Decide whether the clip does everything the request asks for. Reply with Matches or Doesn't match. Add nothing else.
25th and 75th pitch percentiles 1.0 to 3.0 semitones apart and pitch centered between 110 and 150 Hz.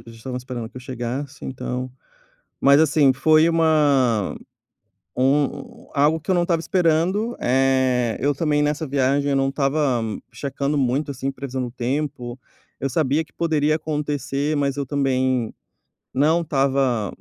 Matches